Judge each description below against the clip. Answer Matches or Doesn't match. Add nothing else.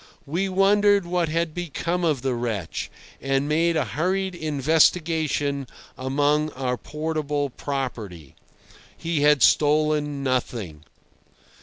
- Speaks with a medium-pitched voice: Matches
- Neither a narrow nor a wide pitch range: Matches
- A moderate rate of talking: Doesn't match